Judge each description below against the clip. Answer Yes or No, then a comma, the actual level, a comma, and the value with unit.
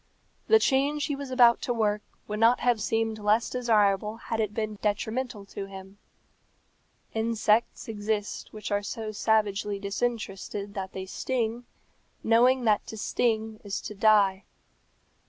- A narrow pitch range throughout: Yes, narrow, 2.3 semitones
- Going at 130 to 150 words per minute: Yes, average, 140 wpm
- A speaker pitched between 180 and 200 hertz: No, high, 215 Hz